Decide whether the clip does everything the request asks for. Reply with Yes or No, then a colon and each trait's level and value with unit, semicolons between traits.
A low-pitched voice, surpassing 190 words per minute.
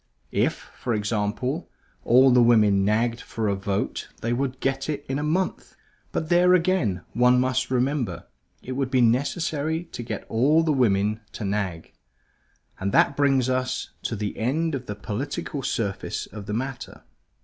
No: low, 125 Hz; average, 165 wpm